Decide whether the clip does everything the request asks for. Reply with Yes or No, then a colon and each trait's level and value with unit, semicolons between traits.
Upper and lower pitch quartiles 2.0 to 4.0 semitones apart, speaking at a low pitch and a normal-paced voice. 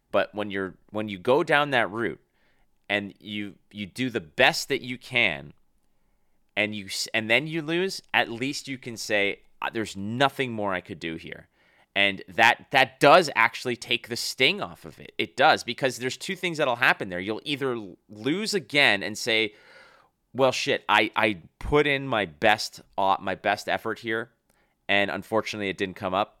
No: average, 4.4 semitones; low, 110 Hz; average, 180 wpm